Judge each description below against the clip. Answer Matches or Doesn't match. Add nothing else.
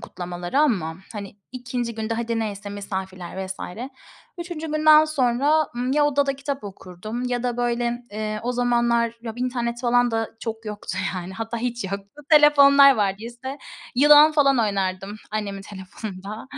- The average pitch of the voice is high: Matches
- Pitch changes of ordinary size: Matches